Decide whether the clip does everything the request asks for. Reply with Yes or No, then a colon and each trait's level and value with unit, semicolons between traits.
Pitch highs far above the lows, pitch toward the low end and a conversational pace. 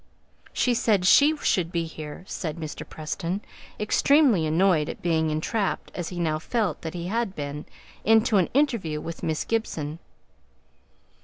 No: wide, 5.7 semitones; medium, 175 Hz; average, 150 wpm